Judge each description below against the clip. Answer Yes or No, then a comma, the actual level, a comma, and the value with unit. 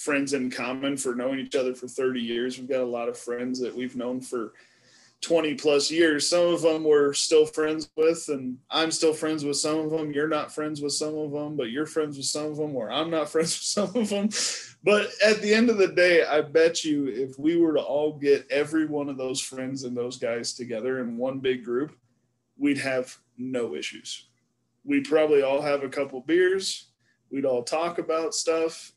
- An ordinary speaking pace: No, fast, 220 wpm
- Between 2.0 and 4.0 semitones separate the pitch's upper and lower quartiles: Yes, average, 3.7 semitones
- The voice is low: No, medium, 145 Hz